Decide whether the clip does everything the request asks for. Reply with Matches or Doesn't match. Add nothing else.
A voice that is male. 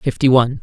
Doesn't match